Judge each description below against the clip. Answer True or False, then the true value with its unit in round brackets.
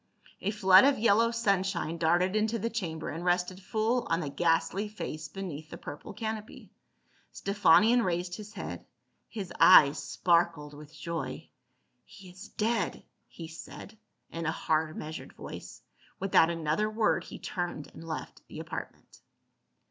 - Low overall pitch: False (180 Hz)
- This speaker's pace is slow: False (150 wpm)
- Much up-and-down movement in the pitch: False (4.6 semitones)